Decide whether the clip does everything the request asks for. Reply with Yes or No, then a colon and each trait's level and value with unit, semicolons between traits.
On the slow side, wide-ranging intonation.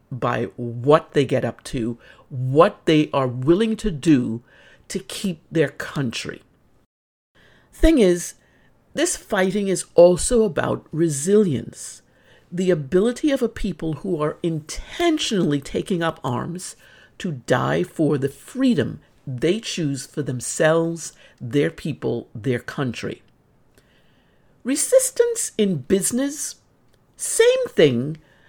Yes: slow, 110 wpm; wide, 6.7 semitones